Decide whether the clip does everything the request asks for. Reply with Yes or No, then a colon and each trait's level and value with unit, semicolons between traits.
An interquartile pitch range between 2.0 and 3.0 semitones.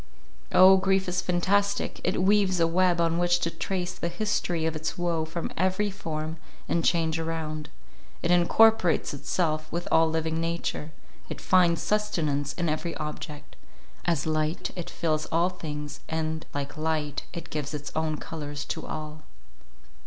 Yes: narrow, 2.4 semitones